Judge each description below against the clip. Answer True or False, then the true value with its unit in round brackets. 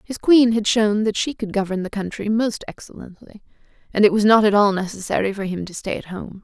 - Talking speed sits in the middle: False (235 wpm)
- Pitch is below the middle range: False (205 Hz)